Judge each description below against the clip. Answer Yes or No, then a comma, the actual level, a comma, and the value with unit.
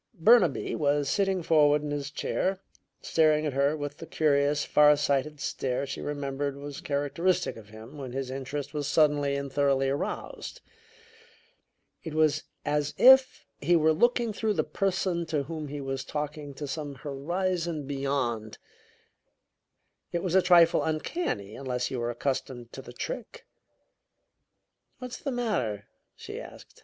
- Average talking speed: Yes, average, 150 wpm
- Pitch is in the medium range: Yes, medium, 145 Hz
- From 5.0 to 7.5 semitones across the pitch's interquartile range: No, average, 3.4 semitones